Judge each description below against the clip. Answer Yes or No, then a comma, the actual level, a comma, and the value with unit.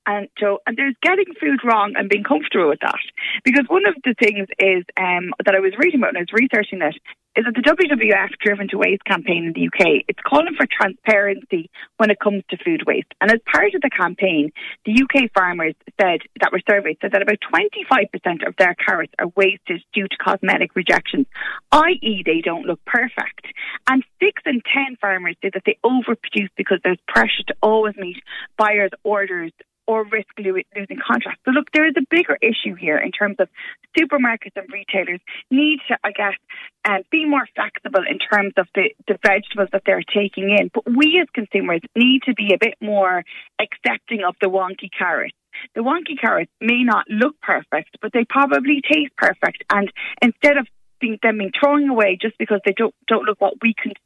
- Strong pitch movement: Yes, wide, 6.1 semitones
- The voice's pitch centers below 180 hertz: No, high, 220 Hz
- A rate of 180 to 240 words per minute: Yes, average, 200 wpm